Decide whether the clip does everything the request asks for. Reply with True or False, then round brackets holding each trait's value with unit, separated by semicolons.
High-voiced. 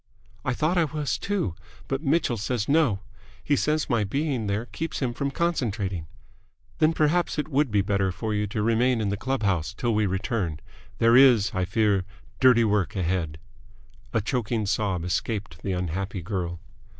False (110 Hz)